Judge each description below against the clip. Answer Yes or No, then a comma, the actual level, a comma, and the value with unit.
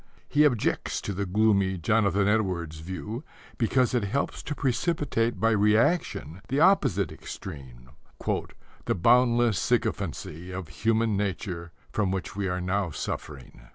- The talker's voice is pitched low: Yes, low, 100 Hz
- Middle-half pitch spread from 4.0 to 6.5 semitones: Yes, average, 4.4 semitones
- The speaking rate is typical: No, slow, 130 wpm